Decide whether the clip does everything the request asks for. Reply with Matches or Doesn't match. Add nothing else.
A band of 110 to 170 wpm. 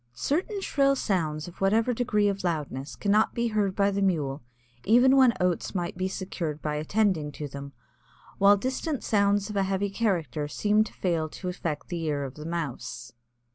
Doesn't match